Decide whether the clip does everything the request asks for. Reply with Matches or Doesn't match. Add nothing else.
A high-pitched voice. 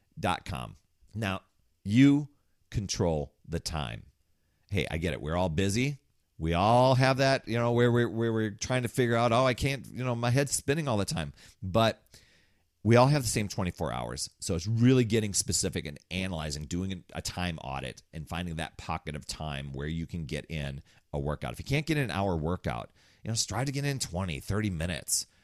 Doesn't match